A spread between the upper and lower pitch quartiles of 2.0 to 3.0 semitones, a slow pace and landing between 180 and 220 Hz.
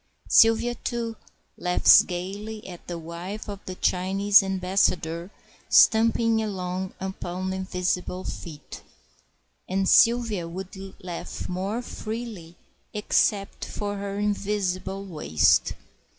Yes: narrow, 2.6 semitones; slow, 100 wpm; high, 190 Hz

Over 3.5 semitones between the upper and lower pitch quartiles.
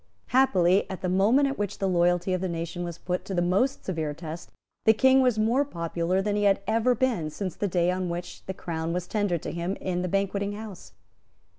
No: average, 3.2 semitones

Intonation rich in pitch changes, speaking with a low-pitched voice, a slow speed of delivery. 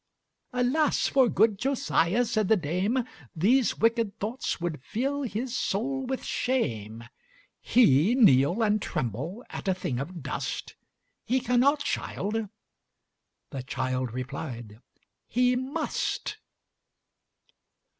No: wide, 9.0 semitones; high, 215 Hz; slow, 110 wpm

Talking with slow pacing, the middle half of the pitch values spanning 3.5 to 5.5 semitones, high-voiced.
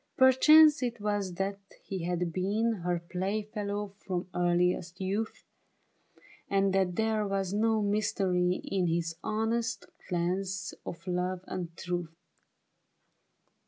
No: slow, 120 wpm; average, 3.1 semitones; high, 195 Hz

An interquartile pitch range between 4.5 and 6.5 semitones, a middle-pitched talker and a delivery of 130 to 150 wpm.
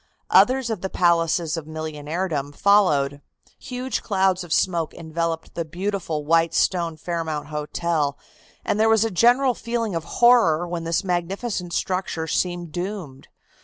No: average, 3.7 semitones; medium, 170 Hz; average, 140 wpm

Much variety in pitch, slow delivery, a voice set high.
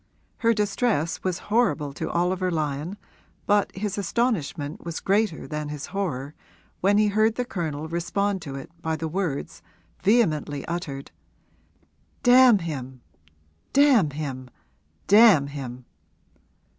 No: wide, 5.9 semitones; slow, 120 wpm; medium, 170 Hz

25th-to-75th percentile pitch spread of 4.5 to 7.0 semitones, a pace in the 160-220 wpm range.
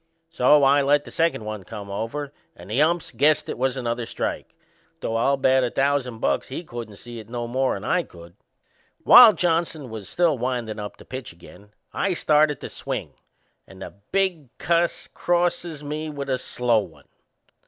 Yes: average, 5.3 semitones; average, 180 wpm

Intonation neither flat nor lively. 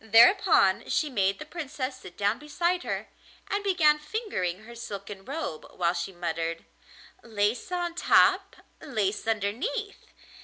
No: wide, 8.8 semitones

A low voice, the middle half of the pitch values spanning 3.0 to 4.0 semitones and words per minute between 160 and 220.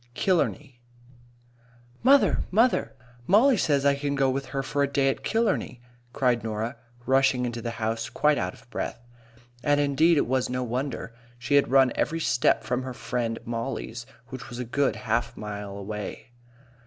Yes: low, 130 Hz; average, 3.5 semitones; average, 165 wpm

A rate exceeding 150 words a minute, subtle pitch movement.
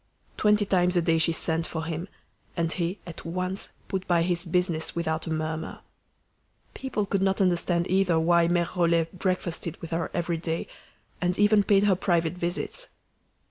Yes: average, 170 wpm; narrow, 2.1 semitones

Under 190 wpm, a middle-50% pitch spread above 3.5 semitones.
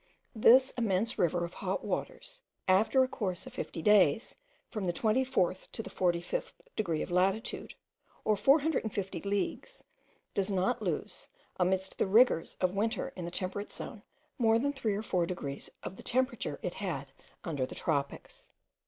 Yes: average, 160 wpm; average, 4.4 semitones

